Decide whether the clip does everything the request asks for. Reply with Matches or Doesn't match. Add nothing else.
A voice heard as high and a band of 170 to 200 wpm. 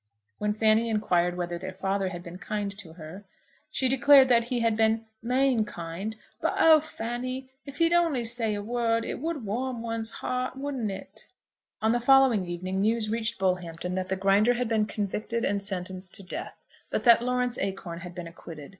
Matches